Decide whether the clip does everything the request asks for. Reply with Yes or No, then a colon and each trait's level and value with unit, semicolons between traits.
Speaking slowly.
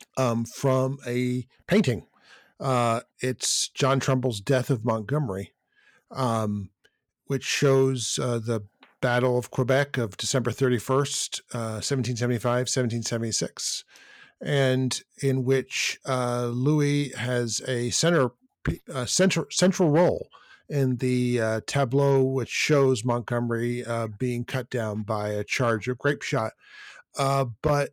Yes: slow, 120 wpm